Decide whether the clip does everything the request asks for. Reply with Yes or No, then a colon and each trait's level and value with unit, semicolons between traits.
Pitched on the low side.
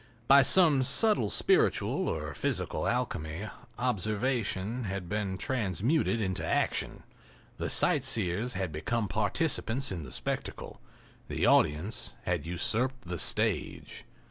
Yes: low, 105 Hz